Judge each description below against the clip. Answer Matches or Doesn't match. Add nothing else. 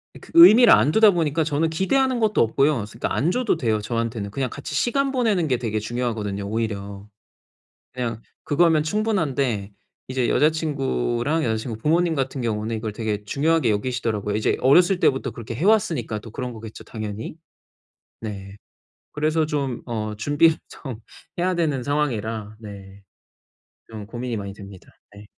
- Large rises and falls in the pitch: Matches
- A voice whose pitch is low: Matches